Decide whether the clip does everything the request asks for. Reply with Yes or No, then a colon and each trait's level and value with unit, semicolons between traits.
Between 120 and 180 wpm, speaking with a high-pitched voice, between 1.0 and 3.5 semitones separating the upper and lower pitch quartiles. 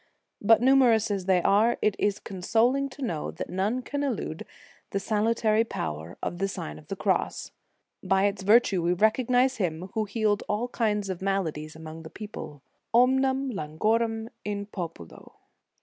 No: average, 165 wpm; high, 205 Hz; average, 4.3 semitones